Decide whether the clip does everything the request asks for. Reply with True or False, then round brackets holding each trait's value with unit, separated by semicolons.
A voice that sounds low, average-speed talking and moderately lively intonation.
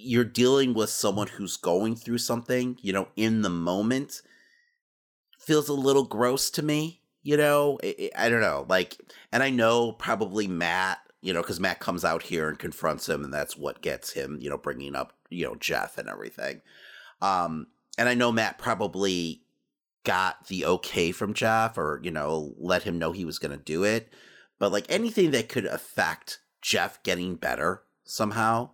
False (110 Hz; 185 wpm; 6.2 semitones)